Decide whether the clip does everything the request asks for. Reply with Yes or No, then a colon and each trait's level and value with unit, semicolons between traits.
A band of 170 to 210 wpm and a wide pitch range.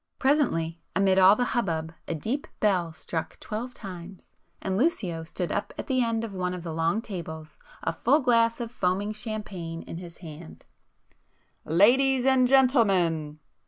No: average, 160 wpm; wide, 6.2 semitones